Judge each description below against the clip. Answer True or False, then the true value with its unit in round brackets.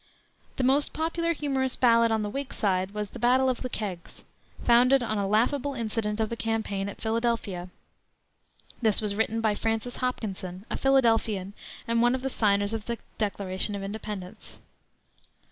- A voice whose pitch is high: True (225 Hz)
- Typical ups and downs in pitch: True (3.4 semitones)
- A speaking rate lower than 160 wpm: False (165 wpm)